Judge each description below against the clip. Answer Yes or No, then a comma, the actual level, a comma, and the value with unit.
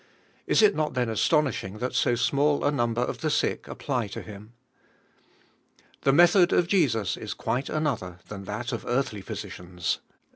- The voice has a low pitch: Yes, low, 120 Hz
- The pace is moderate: Yes, average, 170 wpm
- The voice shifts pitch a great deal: Yes, wide, 5.9 semitones